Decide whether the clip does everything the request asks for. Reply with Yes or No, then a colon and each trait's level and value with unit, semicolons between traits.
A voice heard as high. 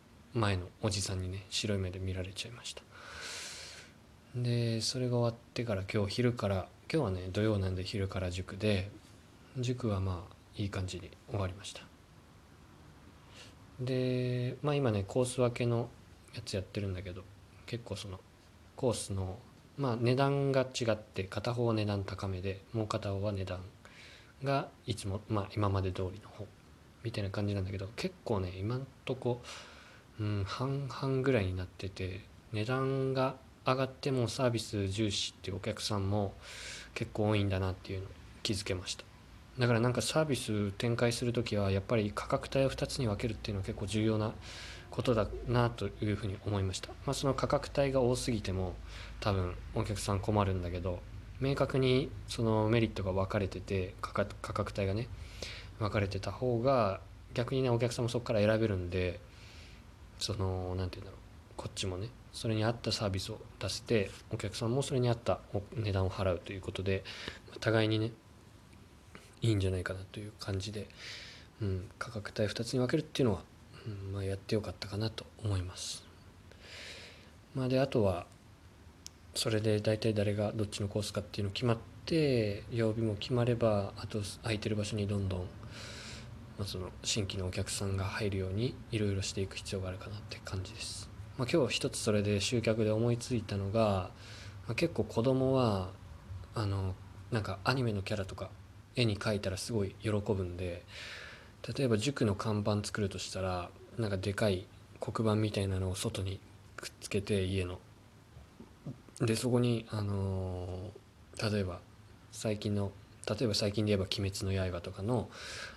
No: low, 105 Hz